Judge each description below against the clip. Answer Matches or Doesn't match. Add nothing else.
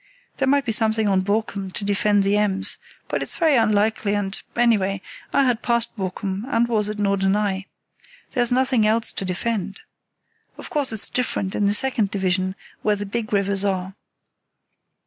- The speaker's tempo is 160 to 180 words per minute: Matches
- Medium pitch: Doesn't match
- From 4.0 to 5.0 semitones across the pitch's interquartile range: Doesn't match